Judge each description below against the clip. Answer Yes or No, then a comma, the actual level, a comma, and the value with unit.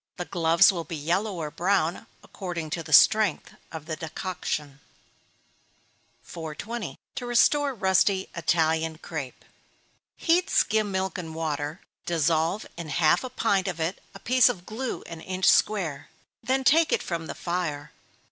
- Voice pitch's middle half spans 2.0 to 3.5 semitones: No, average, 4.3 semitones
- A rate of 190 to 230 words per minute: No, average, 145 wpm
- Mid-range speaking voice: Yes, medium, 175 Hz